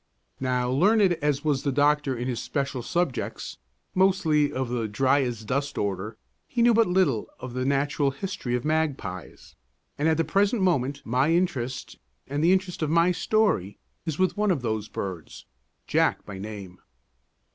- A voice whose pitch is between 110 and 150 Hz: Yes, medium, 140 Hz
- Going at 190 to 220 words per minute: No, average, 170 wpm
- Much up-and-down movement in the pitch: Yes, wide, 5.9 semitones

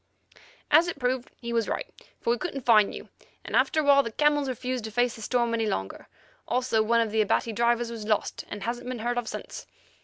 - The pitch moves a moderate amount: No, narrow, 2.3 semitones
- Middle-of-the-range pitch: No, high, 235 Hz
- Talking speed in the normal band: No, fast, 220 wpm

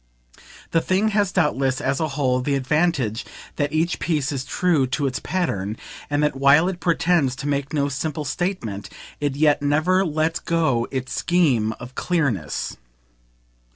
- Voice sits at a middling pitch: Yes, medium, 145 Hz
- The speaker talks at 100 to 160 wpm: Yes, average, 155 wpm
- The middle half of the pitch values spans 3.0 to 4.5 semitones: Yes, average, 4.0 semitones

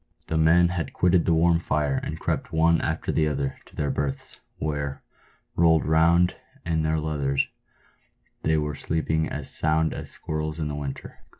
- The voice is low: Yes, very low, 80 Hz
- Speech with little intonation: Yes, narrow, 1.8 semitones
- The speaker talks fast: No, average, 165 wpm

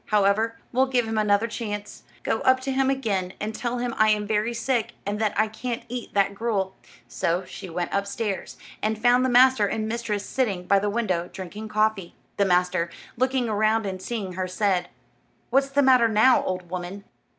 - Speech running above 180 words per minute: Yes, average, 190 wpm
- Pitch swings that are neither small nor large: Yes, average, 3.3 semitones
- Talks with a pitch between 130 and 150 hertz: No, high, 215 Hz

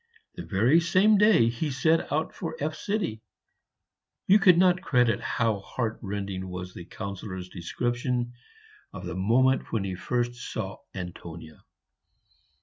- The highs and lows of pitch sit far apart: Yes, wide, 8.0 semitones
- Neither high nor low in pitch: No, low, 115 Hz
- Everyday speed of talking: No, slow, 130 wpm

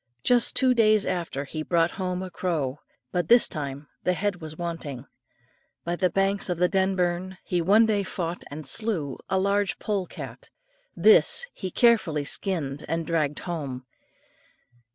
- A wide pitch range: No, average, 3.9 semitones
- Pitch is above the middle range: No, medium, 180 Hz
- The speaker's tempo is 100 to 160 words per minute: Yes, average, 155 wpm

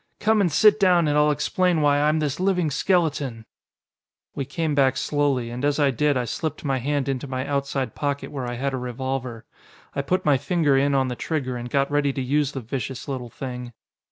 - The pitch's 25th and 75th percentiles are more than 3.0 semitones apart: No, narrow, 2.6 semitones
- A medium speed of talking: No, fast, 215 wpm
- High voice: No, medium, 140 Hz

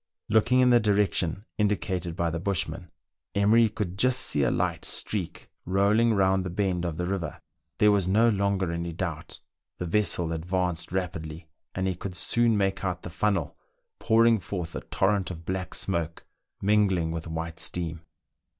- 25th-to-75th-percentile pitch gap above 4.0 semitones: No, average, 3.5 semitones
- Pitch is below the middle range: Yes, very low, 95 Hz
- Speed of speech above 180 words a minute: No, average, 165 wpm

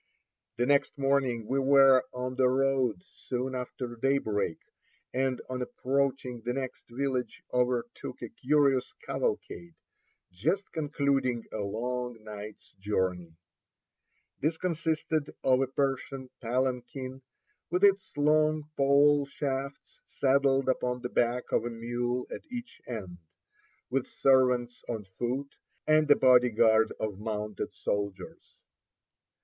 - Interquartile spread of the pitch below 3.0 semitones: Yes, narrow, 2.6 semitones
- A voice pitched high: No, low, 130 Hz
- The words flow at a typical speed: No, slow, 120 wpm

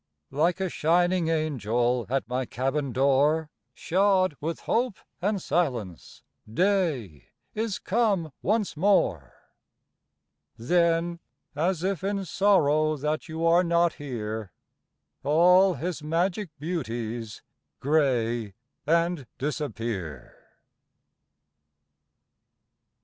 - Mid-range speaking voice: Yes, medium, 155 Hz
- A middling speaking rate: No, slow, 90 wpm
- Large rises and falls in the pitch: Yes, wide, 6.0 semitones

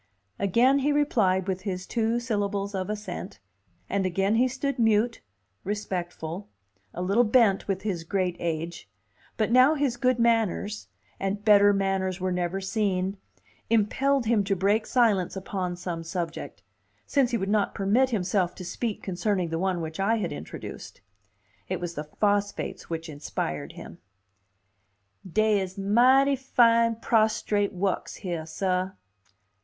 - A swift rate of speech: No, average, 145 wpm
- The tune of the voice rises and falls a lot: No, average, 3.8 semitones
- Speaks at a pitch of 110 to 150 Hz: No, high, 200 Hz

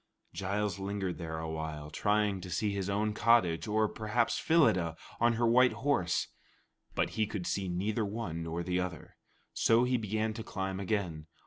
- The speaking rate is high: No, average, 175 wpm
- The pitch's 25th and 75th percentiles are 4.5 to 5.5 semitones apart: No, average, 3.8 semitones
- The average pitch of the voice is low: Yes, low, 100 Hz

